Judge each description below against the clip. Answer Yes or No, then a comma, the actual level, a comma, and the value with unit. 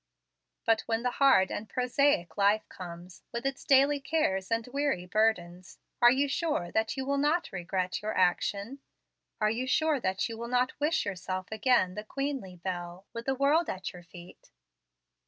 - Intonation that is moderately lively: No, wide, 6.6 semitones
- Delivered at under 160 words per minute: No, average, 175 wpm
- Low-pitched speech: No, high, 225 Hz